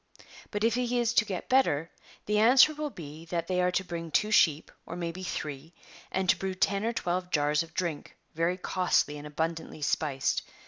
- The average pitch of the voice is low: No, medium, 180 Hz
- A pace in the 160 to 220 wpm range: Yes, average, 200 wpm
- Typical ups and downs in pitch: Yes, average, 4.5 semitones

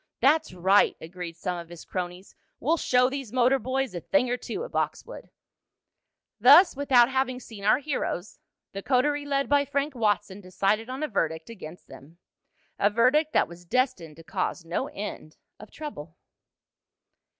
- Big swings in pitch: Yes, wide, 7.1 semitones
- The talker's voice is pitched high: Yes, high, 230 Hz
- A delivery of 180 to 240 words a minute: No, average, 160 wpm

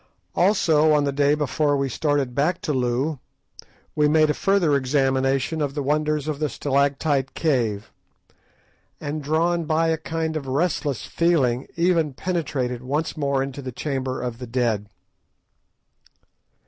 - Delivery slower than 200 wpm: Yes, average, 145 wpm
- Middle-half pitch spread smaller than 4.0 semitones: Yes, average, 2.8 semitones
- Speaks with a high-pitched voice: No, medium, 145 Hz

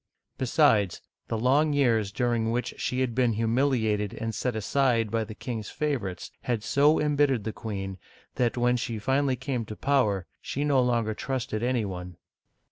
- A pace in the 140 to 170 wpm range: Yes, average, 165 wpm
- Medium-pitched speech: No, low, 120 Hz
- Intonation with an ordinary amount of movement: Yes, average, 3.5 semitones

